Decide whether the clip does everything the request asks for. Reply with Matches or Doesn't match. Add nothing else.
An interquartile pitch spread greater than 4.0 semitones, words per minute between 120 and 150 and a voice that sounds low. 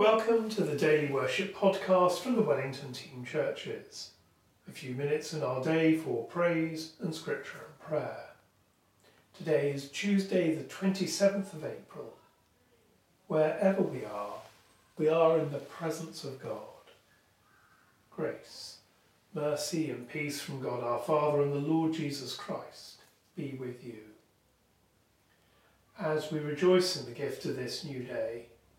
Doesn't match